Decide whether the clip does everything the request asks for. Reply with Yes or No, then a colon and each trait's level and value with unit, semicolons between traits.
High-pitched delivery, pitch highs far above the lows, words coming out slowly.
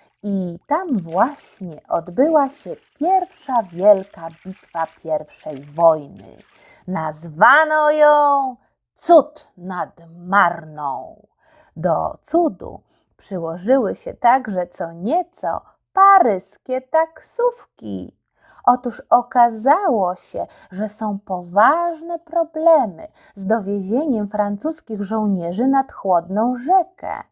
Yes: high, 220 Hz; wide, 8.4 semitones; slow, 85 wpm